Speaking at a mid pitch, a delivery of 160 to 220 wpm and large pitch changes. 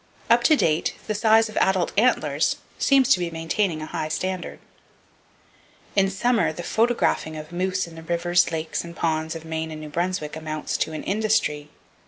No: medium, 175 Hz; average, 180 wpm; average, 4.6 semitones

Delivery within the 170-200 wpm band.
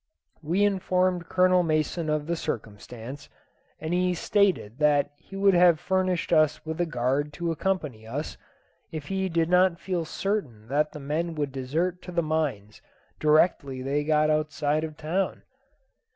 No: average, 155 wpm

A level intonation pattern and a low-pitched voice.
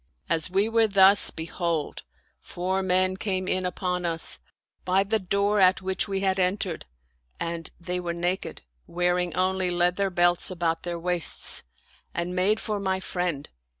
No: narrow, 1.6 semitones; medium, 180 Hz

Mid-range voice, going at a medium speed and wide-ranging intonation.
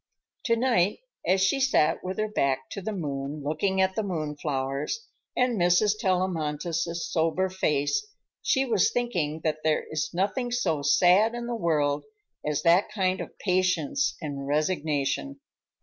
Yes: medium, 180 Hz; average, 150 wpm; wide, 5.9 semitones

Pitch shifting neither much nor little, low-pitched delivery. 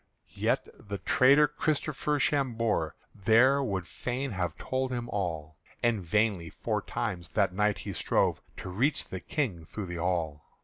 No: wide, 6.6 semitones; low, 105 Hz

